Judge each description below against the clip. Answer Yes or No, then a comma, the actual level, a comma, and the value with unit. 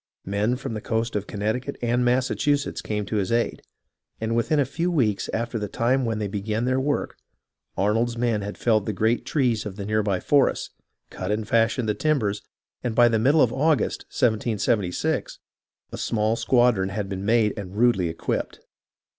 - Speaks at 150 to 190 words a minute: Yes, average, 185 wpm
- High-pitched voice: No, low, 115 Hz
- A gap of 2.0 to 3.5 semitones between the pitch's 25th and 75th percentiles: Yes, average, 2.9 semitones